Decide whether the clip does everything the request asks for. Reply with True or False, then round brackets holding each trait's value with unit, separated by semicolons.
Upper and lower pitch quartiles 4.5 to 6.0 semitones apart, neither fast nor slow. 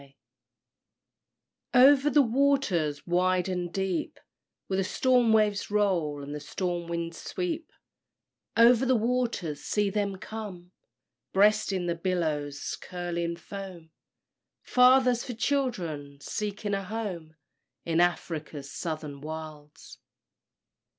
False (5.3 semitones; 110 wpm)